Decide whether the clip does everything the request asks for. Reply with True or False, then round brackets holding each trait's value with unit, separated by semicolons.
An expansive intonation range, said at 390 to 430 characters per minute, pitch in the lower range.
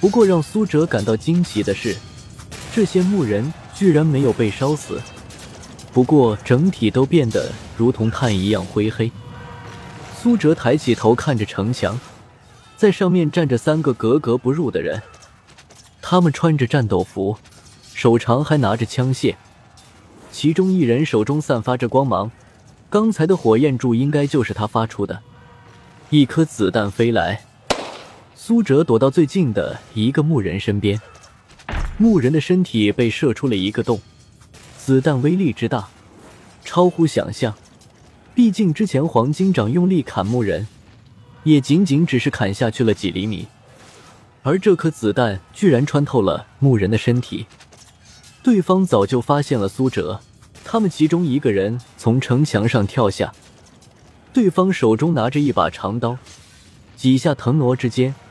False (5.9 semitones; 220 characters per minute; 125 Hz)